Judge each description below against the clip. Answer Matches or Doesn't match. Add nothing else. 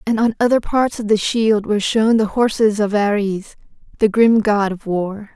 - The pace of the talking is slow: Doesn't match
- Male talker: Doesn't match